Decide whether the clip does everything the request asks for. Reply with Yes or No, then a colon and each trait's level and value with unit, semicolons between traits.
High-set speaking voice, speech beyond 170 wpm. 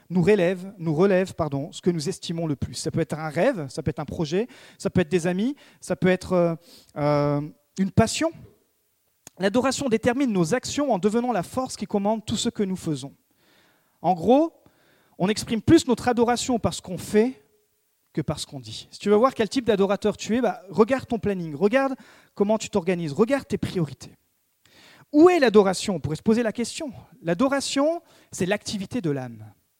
Yes: high, 200 Hz; average, 195 wpm